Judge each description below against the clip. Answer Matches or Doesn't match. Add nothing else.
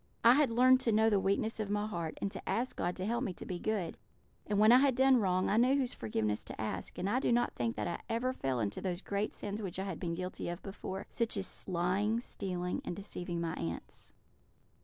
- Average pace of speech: Doesn't match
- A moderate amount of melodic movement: Matches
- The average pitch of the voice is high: Matches